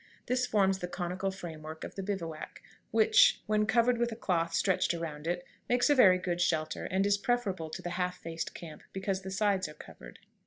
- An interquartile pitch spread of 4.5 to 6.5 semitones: No, average, 3.9 semitones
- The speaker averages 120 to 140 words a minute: No, fast, 205 wpm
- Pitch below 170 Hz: No, high, 190 Hz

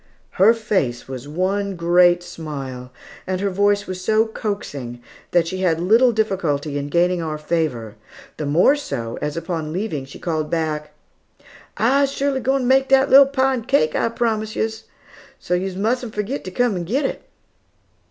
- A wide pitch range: Yes, wide, 6.3 semitones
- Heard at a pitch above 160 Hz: Yes, medium, 185 Hz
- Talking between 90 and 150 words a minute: No, average, 170 wpm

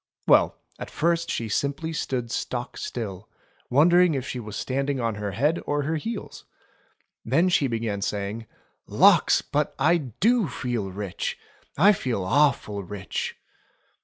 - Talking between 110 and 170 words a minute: Yes, average, 140 wpm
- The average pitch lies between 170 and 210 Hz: No, low, 125 Hz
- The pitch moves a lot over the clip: Yes, wide, 6.7 semitones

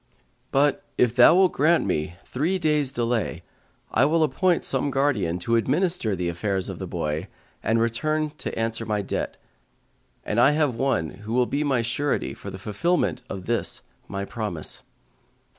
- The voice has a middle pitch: No, low, 120 Hz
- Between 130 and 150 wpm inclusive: No, average, 165 wpm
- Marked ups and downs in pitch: Yes, wide, 6.2 semitones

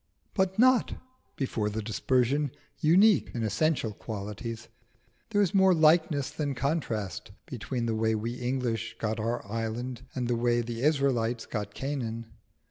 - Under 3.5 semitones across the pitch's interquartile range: No, average, 4.5 semitones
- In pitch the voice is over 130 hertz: No, low, 120 Hz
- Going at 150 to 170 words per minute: No, average, 140 wpm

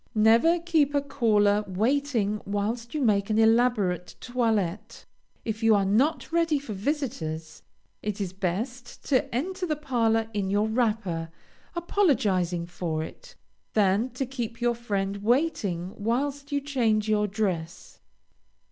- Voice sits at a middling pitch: No, high, 225 Hz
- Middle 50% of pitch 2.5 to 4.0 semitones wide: No, average, 5.1 semitones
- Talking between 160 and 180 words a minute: No, slow, 135 wpm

